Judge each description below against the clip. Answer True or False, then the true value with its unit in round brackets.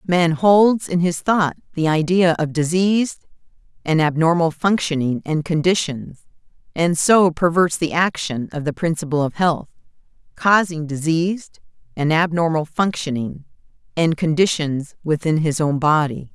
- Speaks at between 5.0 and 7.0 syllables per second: False (4.5 syllables/s)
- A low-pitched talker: False (165 Hz)